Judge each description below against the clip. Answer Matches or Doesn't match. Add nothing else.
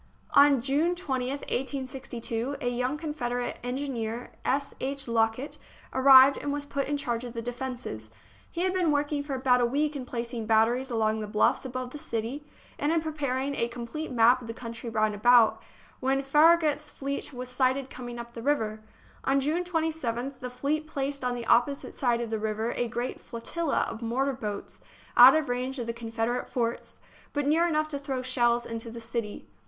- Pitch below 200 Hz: Doesn't match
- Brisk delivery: Doesn't match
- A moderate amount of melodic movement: Matches